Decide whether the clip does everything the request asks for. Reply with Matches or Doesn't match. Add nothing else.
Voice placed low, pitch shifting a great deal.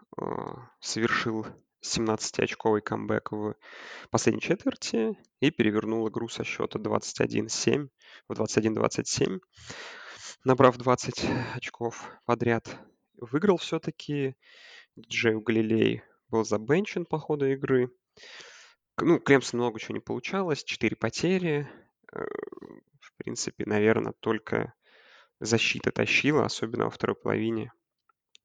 Matches